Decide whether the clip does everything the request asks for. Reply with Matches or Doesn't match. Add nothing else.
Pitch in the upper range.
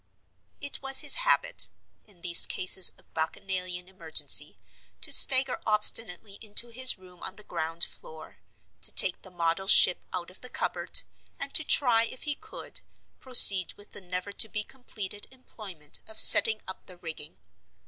Matches